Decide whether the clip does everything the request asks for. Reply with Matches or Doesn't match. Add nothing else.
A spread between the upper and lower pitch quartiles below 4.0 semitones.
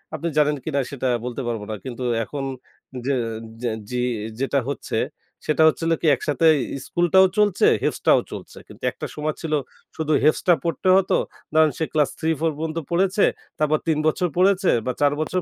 Matches